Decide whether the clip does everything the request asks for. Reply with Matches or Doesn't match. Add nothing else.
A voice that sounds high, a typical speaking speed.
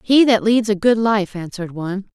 Doesn't match